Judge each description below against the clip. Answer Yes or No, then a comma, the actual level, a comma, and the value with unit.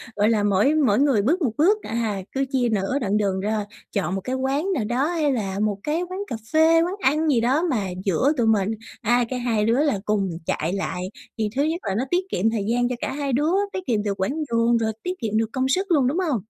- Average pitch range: No, wide, 5.9 semitones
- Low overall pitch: No, high, 240 Hz